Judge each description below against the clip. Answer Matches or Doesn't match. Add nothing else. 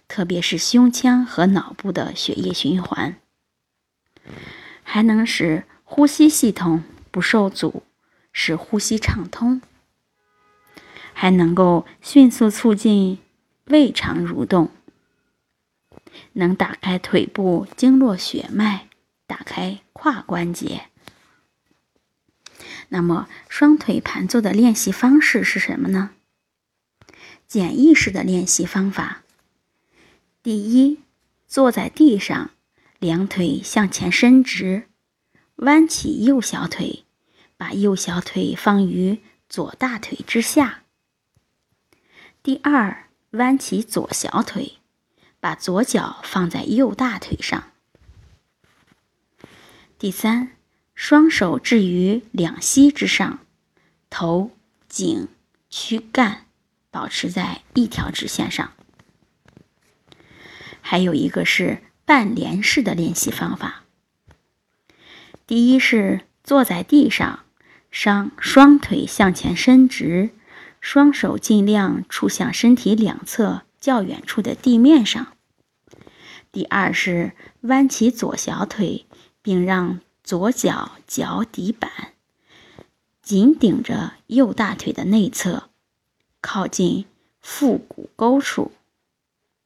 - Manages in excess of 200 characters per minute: Doesn't match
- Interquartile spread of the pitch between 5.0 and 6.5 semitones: Matches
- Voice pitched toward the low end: Doesn't match